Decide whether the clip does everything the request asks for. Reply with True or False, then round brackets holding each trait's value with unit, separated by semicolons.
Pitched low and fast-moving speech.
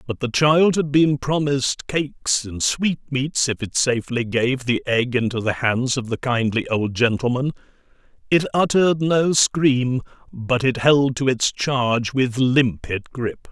False (130 Hz; 160 wpm)